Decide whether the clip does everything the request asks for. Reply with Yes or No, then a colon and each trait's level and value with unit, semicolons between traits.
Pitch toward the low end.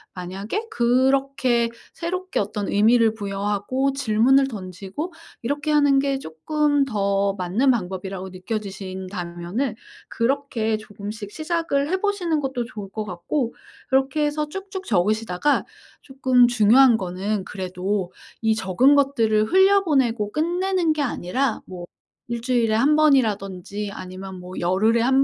No: high, 230 Hz